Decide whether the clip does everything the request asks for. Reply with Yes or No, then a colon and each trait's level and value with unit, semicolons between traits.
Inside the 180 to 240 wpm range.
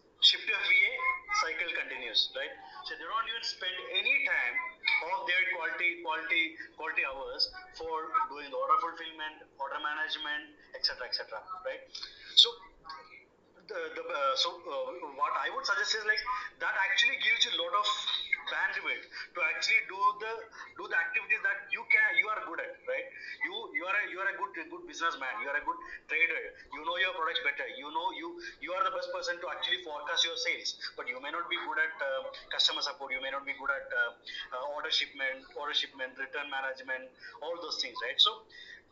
Yes: average, 190 wpm